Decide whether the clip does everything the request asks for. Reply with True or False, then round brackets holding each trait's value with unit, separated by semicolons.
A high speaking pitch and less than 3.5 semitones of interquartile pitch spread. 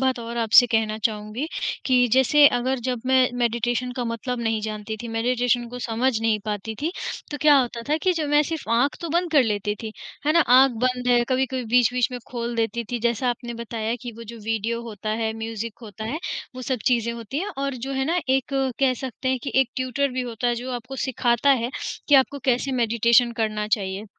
True (240 Hz; 2.5 semitones)